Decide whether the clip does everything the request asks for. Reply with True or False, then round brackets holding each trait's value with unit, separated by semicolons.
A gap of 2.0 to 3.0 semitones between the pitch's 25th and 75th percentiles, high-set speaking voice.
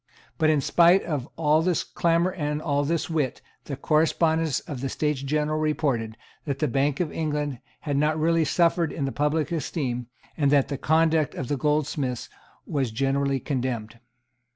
False (2.6 semitones; 150 Hz)